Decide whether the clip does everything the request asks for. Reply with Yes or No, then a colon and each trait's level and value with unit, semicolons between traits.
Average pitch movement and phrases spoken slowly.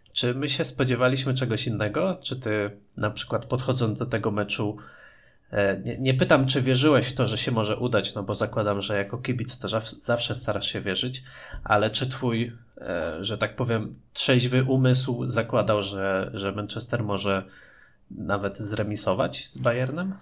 No: average, 3.5 semitones; average, 155 wpm